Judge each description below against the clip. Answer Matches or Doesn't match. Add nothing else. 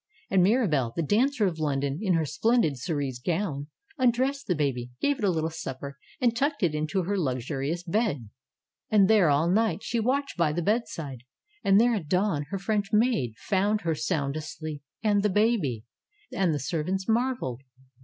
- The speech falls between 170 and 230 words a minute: Matches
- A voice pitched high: Doesn't match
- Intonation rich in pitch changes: Matches